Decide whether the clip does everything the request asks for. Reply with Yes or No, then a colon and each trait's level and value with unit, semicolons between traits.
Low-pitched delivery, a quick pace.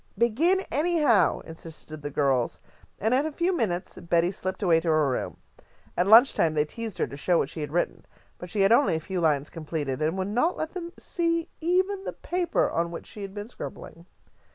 No: high, 190 Hz; fast, 215 wpm